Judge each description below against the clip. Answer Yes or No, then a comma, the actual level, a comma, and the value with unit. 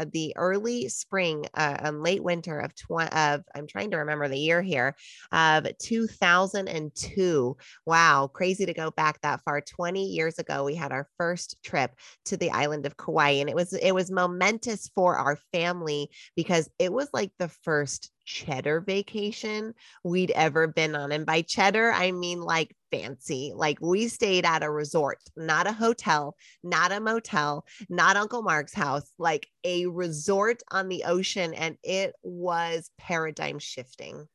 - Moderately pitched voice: Yes, medium, 170 Hz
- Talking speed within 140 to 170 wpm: Yes, average, 165 wpm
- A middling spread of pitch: Yes, average, 3.6 semitones